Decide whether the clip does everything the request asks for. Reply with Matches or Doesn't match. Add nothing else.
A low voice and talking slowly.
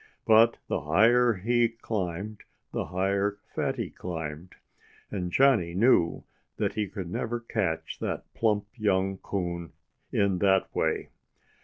Matches